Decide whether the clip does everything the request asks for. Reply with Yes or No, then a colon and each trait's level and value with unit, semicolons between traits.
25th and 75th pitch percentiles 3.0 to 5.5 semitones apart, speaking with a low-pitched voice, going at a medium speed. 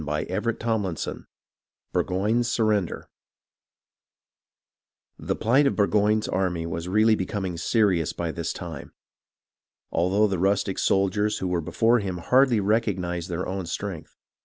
No: average, 3.6 semitones; very low, 95 Hz; slow, 120 wpm